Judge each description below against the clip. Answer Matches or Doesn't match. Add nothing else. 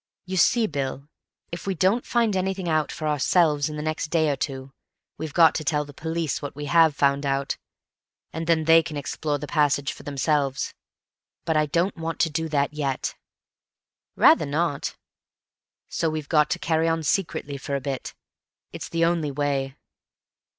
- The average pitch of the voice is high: Doesn't match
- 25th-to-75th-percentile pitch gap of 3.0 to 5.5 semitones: Doesn't match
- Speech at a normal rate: Matches